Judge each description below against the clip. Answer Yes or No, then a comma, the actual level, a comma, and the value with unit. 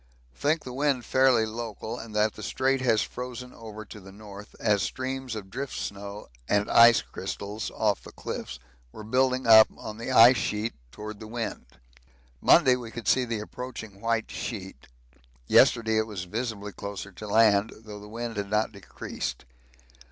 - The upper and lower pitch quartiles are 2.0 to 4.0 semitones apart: Yes, average, 2.7 semitones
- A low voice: Yes, low, 110 Hz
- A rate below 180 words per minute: Yes, average, 165 wpm